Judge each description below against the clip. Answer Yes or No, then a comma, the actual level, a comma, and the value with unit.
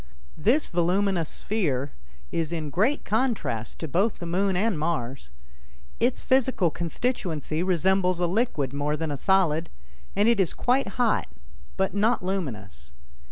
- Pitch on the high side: No, medium, 180 Hz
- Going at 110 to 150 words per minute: Yes, average, 140 wpm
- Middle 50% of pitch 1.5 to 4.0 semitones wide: No, average, 5.3 semitones